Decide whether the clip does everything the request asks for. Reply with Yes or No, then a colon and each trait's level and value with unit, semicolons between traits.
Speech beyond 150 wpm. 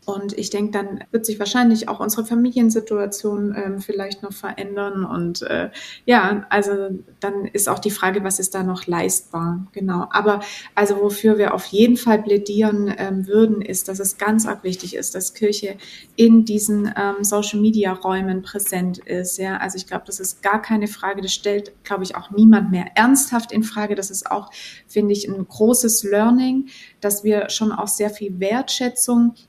Yes: average, 180 wpm